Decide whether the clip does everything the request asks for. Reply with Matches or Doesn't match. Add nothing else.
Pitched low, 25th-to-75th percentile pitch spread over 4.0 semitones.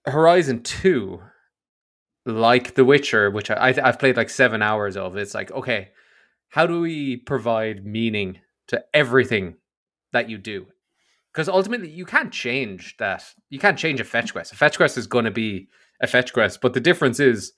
Matches